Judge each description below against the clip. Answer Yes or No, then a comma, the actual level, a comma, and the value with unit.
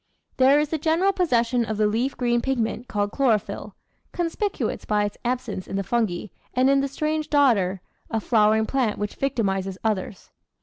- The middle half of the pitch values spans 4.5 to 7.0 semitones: Yes, average, 4.8 semitones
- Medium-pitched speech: No, high, 240 Hz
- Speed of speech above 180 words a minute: No, average, 175 wpm